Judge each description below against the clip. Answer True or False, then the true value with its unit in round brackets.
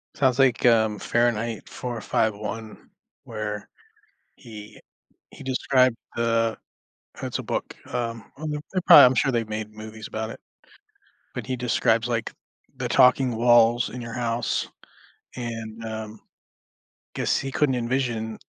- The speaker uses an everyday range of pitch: False (2.1 semitones)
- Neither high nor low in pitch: False (115 Hz)